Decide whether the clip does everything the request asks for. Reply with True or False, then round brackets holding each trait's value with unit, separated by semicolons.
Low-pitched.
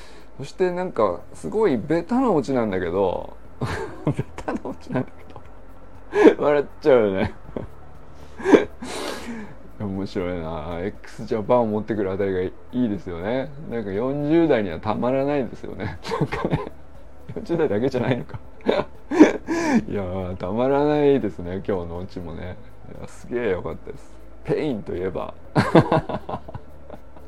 True (105 Hz)